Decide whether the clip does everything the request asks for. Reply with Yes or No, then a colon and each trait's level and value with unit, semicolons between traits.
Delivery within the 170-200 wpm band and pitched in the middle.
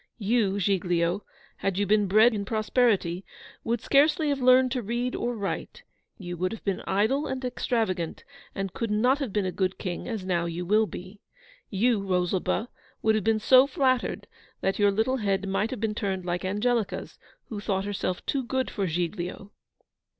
No: average, 180 wpm; high, 205 Hz